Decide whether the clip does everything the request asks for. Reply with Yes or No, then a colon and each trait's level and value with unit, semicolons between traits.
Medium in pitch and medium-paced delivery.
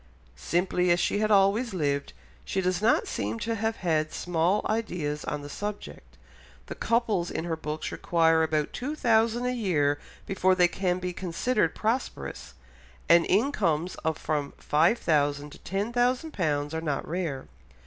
Yes: medium, 180 Hz; average, 160 wpm